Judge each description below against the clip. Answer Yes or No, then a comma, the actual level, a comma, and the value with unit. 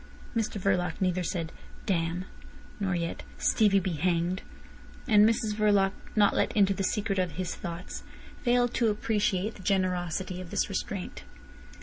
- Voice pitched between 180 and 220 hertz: Yes, high, 190 Hz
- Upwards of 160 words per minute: No, average, 145 wpm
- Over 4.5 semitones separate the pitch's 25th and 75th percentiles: No, average, 2.7 semitones